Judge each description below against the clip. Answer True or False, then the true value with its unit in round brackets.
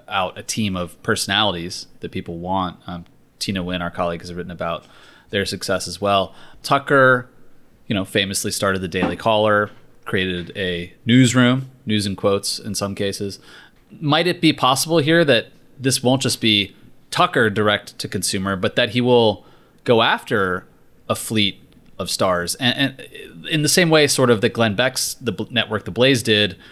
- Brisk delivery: False (175 wpm)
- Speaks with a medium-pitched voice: False (105 Hz)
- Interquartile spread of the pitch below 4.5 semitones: False (5.0 semitones)